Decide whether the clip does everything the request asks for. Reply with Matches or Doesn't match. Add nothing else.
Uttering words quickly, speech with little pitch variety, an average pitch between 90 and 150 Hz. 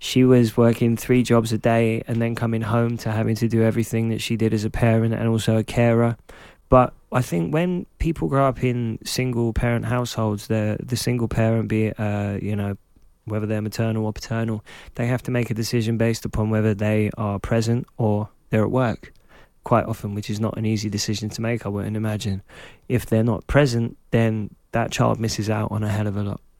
Matches